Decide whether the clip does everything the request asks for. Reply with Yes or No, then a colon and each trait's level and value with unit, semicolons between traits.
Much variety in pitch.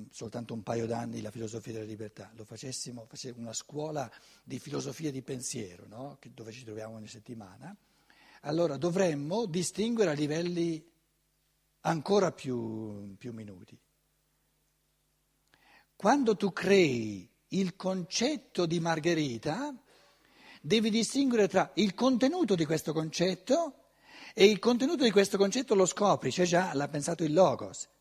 Yes: wide, 8.9 semitones